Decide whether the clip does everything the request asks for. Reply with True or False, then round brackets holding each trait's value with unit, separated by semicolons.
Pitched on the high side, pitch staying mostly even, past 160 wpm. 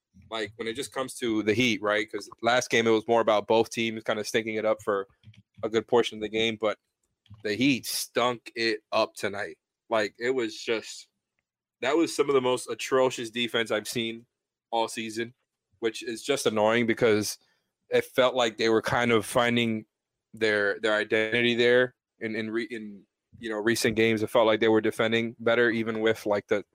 False (115 Hz; 1.6 semitones; 200 wpm)